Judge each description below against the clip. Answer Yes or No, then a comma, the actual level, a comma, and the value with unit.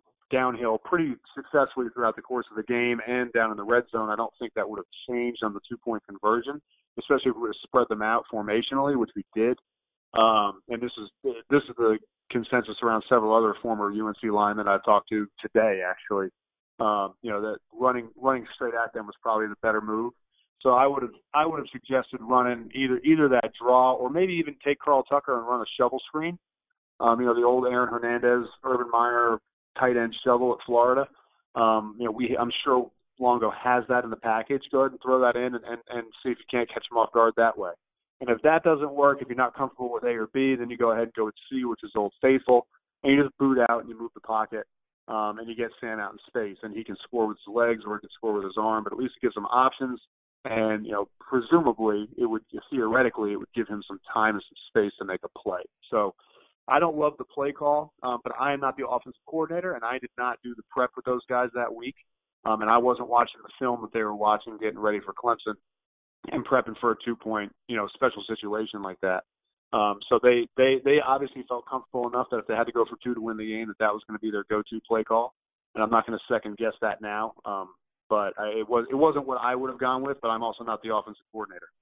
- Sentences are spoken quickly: Yes, fast, 250 wpm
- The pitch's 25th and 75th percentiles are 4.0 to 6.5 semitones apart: No, narrow, 2.6 semitones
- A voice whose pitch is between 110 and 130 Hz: Yes, low, 120 Hz